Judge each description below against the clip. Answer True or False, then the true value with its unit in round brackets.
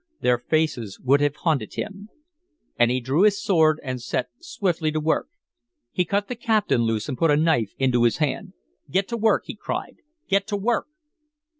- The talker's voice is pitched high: False (155 Hz)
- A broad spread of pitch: True (7.7 semitones)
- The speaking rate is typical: True (185 wpm)